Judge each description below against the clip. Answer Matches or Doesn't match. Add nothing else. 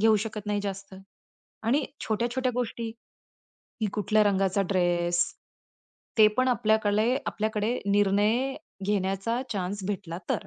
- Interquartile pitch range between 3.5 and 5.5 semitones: Doesn't match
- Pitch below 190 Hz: Doesn't match